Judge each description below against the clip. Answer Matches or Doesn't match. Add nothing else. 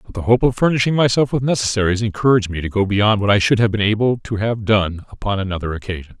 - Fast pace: Matches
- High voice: Doesn't match